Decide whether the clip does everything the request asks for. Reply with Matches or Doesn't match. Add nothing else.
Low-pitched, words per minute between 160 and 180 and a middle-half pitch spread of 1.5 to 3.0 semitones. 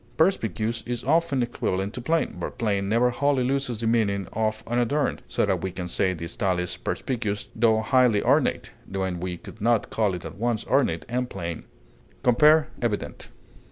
Doesn't match